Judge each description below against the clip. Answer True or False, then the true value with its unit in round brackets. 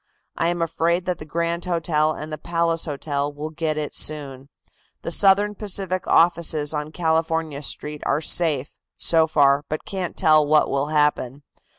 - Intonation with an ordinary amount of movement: False (2.2 semitones)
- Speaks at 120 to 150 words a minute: False (165 wpm)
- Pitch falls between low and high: True (155 Hz)